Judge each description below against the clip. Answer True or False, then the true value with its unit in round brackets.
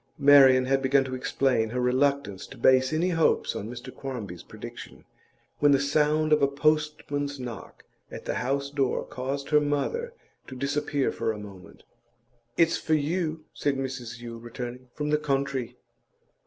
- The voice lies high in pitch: False (135 Hz)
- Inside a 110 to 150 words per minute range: False (160 wpm)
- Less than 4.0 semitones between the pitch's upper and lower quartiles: True (2.8 semitones)